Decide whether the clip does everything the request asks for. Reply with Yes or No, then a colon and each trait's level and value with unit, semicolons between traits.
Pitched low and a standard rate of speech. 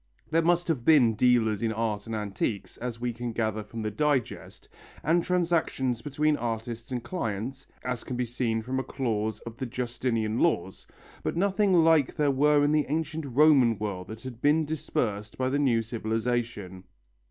Yes: low, 120 Hz; average, 175 wpm